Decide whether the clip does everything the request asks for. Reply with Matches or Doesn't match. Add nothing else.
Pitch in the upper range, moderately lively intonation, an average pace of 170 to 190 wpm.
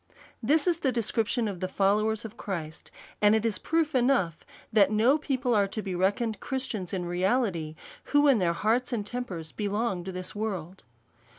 Matches